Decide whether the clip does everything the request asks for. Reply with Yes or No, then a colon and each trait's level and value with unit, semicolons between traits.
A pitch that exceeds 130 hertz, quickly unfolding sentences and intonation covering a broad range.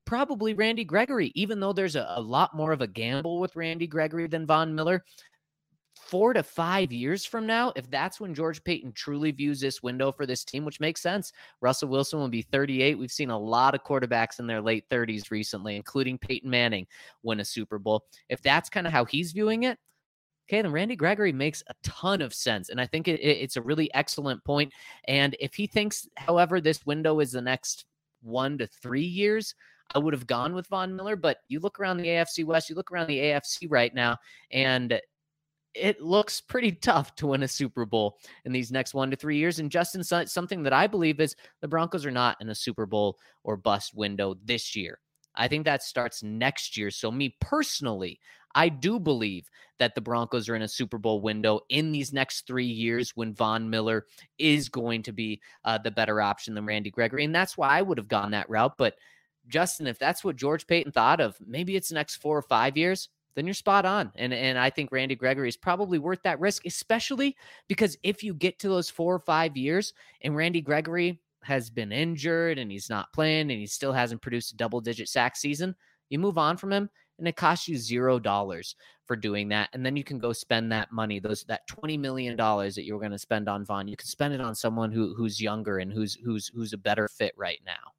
Yes: medium, 140 Hz; fast, 220 wpm; wide, 6.2 semitones